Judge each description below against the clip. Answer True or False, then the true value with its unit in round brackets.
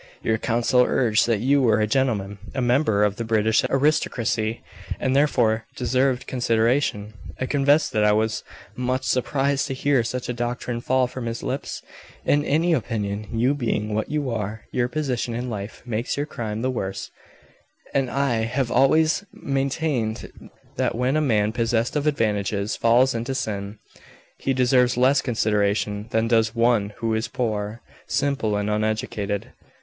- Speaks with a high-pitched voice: False (120 Hz)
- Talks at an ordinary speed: True (160 wpm)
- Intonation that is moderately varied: True (3.3 semitones)